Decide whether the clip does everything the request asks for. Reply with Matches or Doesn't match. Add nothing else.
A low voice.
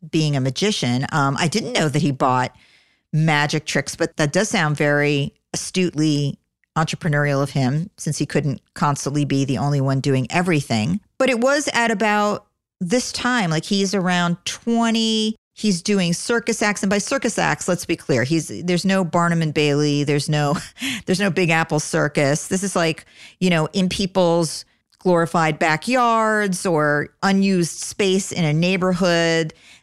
Doesn't match